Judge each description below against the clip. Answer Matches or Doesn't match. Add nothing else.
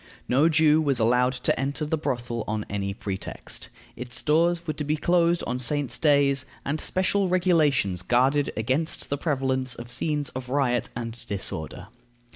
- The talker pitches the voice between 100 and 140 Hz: Matches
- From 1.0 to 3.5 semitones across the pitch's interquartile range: Doesn't match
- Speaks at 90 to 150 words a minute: Doesn't match